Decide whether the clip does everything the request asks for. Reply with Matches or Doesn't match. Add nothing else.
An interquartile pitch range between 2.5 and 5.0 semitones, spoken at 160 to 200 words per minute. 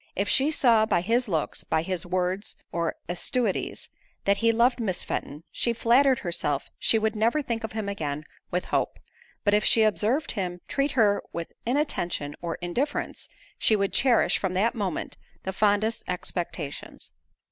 Matches